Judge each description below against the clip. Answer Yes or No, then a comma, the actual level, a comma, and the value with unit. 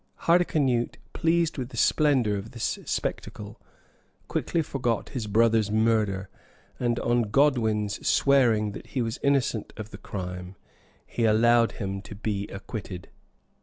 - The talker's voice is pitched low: Yes, low, 115 Hz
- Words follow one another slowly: Yes, slow, 130 wpm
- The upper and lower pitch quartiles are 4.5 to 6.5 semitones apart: No, average, 3.5 semitones